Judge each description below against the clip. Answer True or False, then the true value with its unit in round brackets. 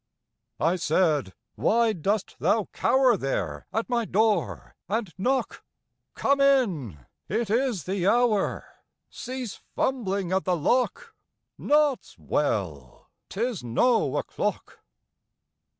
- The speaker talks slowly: True (105 wpm)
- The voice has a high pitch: True (210 Hz)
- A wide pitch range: True (6.9 semitones)